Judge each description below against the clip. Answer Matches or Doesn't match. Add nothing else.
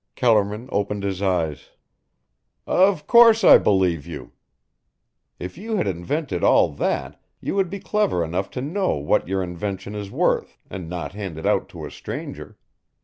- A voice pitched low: Matches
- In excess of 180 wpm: Doesn't match